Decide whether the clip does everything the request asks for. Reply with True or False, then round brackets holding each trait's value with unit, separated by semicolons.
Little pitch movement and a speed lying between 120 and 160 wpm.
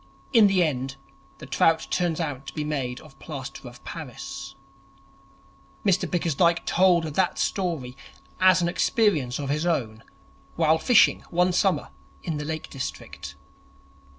False (4.6 semitones; 140 wpm)